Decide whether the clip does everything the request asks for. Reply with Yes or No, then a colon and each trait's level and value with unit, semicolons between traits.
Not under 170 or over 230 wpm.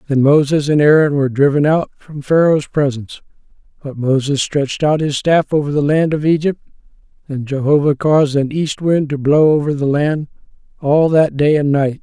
Yes: average, 185 wpm